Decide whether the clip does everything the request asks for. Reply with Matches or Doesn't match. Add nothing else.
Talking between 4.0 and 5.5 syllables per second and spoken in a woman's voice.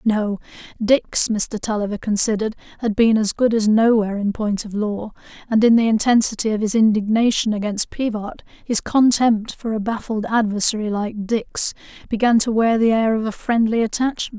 Matches